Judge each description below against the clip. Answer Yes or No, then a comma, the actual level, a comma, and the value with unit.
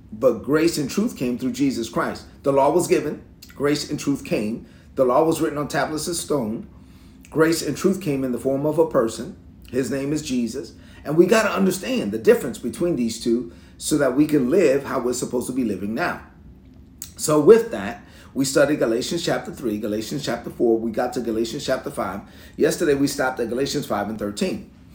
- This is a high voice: No, low, 135 Hz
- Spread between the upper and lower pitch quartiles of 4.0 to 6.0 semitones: Yes, average, 5.2 semitones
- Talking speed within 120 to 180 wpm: No, fast, 205 wpm